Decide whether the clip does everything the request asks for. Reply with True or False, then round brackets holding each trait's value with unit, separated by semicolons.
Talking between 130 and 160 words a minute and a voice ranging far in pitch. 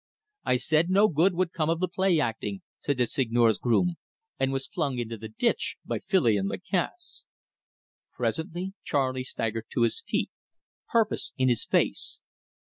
True (155 wpm; 7.1 semitones)